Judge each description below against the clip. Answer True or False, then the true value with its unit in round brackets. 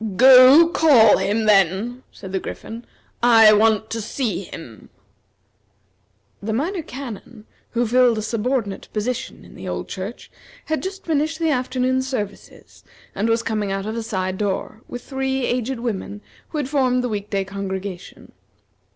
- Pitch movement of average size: True (4.1 semitones)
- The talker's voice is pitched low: False (230 Hz)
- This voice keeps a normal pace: True (155 wpm)